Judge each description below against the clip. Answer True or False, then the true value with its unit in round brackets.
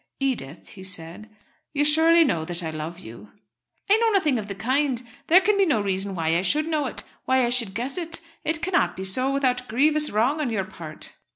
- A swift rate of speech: True (215 wpm)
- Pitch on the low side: False (250 Hz)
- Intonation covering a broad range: True (8.2 semitones)